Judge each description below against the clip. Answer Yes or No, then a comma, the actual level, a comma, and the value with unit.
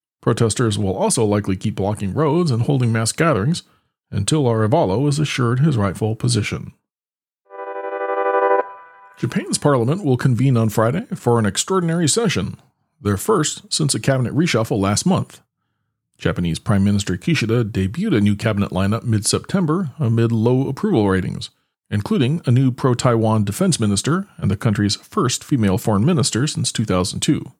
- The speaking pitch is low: Yes, low, 115 Hz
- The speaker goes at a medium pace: Yes, average, 145 wpm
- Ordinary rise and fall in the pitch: No, wide, 6.2 semitones